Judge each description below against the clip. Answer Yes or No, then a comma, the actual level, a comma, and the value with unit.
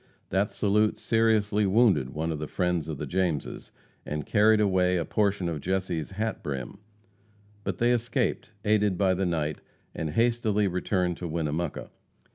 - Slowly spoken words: No, average, 155 wpm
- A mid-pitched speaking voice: No, very low, 95 Hz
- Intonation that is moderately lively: Yes, average, 4.6 semitones